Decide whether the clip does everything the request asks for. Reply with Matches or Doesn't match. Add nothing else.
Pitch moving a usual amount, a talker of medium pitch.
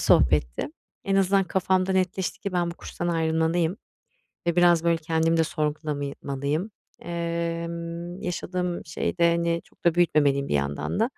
Doesn't match